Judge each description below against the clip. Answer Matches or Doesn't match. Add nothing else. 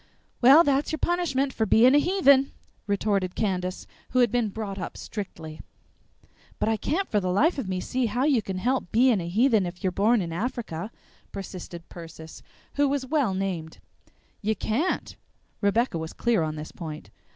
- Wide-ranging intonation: Matches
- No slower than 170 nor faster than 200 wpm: Matches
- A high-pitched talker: Matches